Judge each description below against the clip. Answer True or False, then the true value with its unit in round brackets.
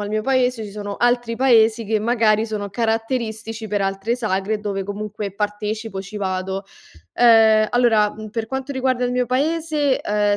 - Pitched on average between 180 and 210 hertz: False (220 Hz)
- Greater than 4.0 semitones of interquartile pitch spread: False (2.8 semitones)